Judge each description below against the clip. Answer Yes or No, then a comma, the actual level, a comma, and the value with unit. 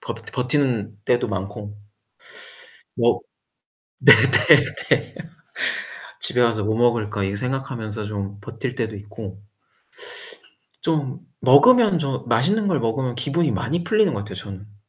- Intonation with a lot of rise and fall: No, average, 4.9 semitones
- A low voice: Yes, low, 120 Hz